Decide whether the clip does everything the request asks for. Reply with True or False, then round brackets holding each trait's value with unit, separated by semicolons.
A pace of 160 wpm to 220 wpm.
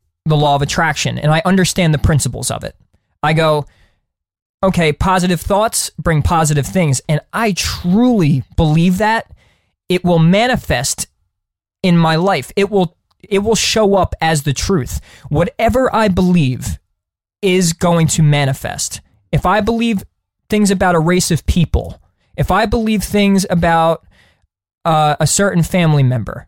False (145 wpm)